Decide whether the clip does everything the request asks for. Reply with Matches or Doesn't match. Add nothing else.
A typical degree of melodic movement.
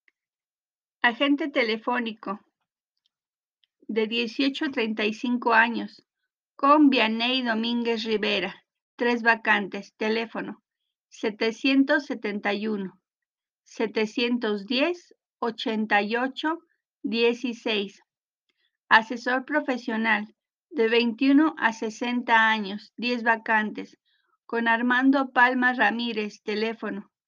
Matches